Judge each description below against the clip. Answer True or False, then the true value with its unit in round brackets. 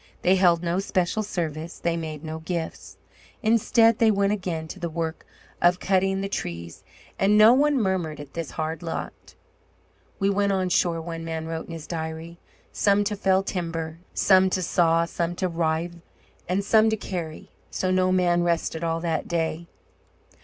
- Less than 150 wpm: False (175 wpm)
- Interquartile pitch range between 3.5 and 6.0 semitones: False (2.8 semitones)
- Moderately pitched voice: True (175 Hz)